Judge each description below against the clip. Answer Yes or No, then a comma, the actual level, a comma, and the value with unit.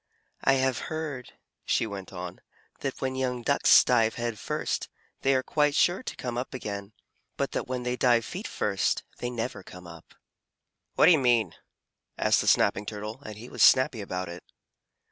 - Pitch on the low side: Yes, low, 120 Hz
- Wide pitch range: No, average, 4.2 semitones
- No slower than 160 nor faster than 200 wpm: Yes, average, 185 wpm